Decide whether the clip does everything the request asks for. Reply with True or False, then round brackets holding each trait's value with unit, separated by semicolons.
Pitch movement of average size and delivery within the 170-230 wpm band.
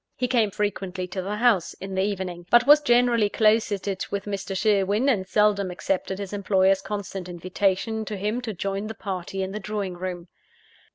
False (2.2 semitones; 180 wpm)